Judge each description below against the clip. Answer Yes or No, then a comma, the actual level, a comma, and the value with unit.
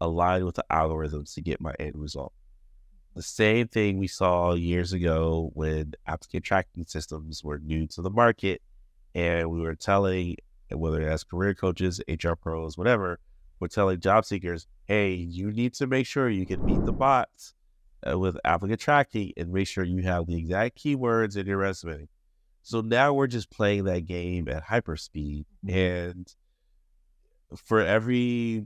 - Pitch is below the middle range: Yes, very low, 90 Hz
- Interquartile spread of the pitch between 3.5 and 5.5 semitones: Yes, average, 3.9 semitones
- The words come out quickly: No, average, 165 wpm